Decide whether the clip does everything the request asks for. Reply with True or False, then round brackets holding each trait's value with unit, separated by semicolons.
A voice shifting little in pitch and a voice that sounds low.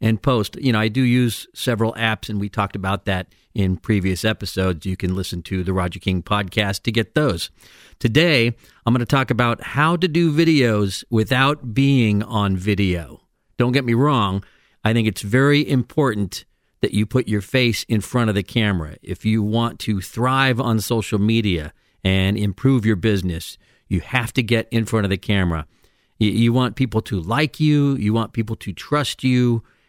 False (4.2 semitones; 110 Hz)